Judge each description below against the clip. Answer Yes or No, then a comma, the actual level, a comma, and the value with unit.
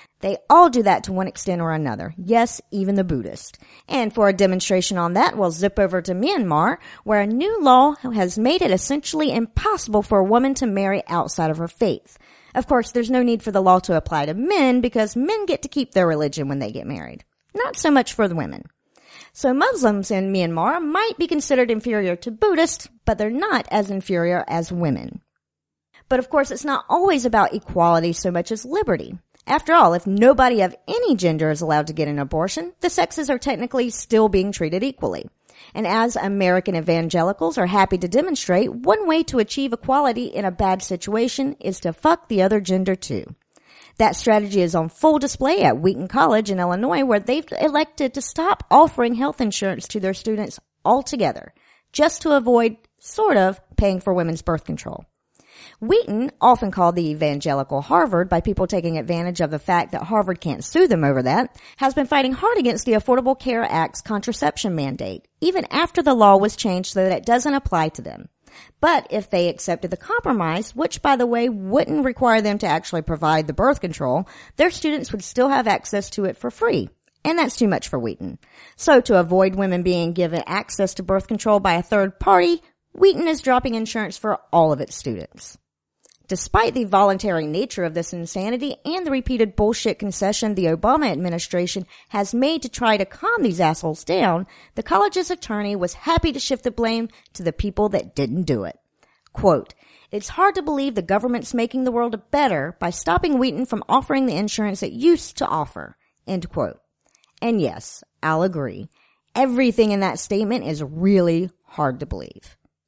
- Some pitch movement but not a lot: No, wide, 6.5 semitones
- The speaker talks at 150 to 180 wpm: No, average, 190 wpm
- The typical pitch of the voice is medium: No, high, 210 Hz